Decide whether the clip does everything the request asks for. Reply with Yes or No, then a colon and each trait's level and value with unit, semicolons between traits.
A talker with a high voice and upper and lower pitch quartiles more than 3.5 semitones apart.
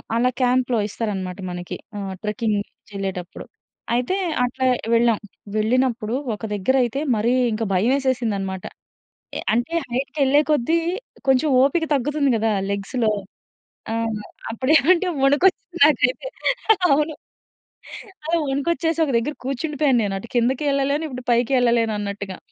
Yes: high, 245 Hz; average, 4.6 semitones